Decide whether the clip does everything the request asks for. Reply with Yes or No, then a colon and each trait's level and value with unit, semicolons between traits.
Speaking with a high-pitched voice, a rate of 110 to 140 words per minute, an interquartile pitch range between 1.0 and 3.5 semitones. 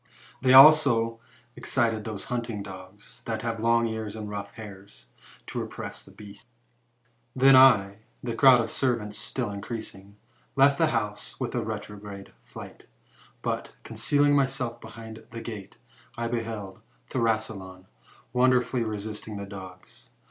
No: low, 110 Hz; slow, 135 wpm; average, 3.0 semitones